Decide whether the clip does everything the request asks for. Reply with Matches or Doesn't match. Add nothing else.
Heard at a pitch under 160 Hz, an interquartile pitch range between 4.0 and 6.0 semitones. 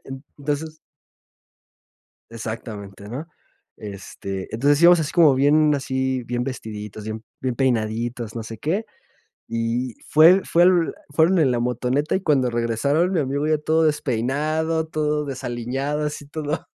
Matches